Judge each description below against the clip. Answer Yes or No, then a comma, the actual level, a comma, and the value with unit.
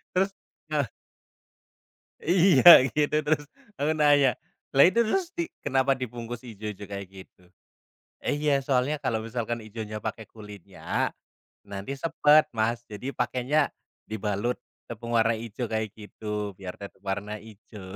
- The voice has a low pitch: Yes, low, 115 Hz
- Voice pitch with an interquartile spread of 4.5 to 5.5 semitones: Yes, average, 5.1 semitones